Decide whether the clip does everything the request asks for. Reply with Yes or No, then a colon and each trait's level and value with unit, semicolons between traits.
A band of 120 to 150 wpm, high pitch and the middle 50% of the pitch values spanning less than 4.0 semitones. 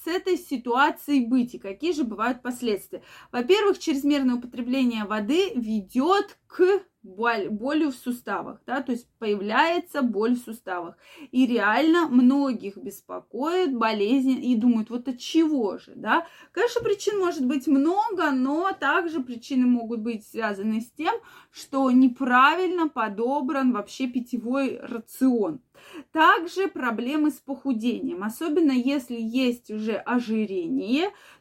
No: average, 125 wpm; very high, 260 Hz; average, 5.0 semitones